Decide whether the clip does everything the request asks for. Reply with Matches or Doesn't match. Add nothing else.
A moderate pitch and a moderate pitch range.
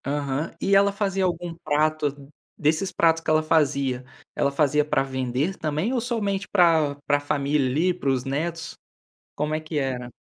Matches